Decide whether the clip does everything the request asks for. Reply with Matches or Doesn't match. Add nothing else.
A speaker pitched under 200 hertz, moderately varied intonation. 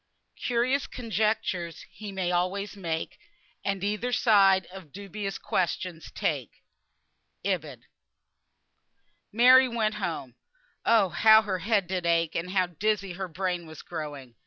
Matches